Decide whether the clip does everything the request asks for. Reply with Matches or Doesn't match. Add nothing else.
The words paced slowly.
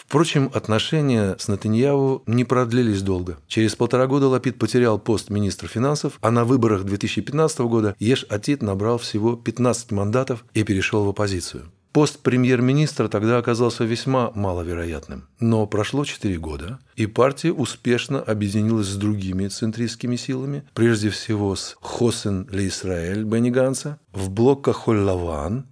Doesn't match